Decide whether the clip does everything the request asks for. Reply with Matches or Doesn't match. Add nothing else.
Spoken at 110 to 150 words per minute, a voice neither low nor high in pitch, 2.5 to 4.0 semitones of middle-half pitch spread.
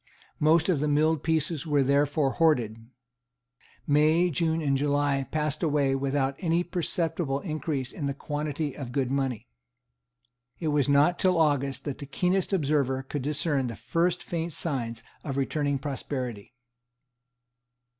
Matches